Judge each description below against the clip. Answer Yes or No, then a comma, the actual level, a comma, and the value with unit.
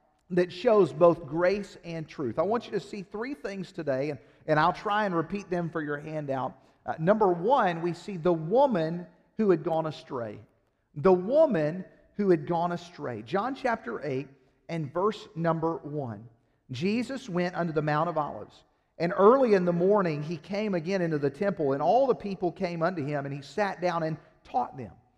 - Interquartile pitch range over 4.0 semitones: Yes, average, 4.4 semitones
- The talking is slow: No, average, 190 wpm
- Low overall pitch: No, medium, 170 Hz